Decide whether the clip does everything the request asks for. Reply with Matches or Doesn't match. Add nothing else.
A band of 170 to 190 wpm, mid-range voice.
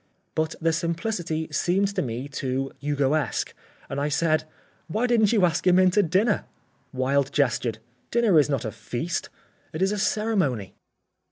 Doesn't match